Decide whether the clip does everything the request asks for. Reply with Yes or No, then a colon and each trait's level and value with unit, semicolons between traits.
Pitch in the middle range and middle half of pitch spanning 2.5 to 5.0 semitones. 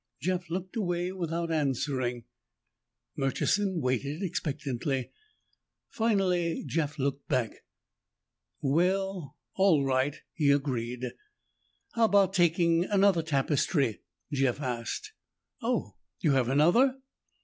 No: medium, 155 Hz; wide, 5.4 semitones